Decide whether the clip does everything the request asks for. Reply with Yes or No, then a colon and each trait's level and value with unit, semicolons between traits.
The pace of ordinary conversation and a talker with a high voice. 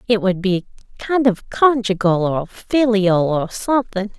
Yes: average, 145 wpm; high, 210 Hz